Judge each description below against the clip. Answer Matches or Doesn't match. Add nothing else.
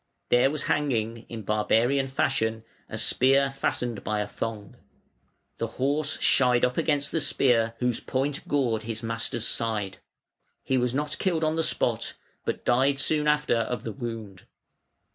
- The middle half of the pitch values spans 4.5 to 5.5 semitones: Doesn't match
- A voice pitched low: Matches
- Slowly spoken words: Doesn't match